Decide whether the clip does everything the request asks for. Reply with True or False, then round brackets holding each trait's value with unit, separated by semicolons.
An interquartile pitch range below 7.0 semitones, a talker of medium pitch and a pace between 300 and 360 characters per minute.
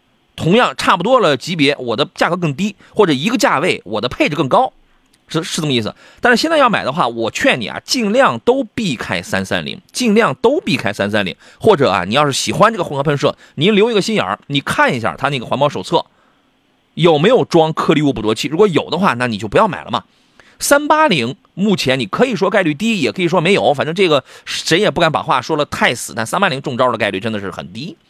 False (7.5 semitones; 180 Hz; 345 characters per minute)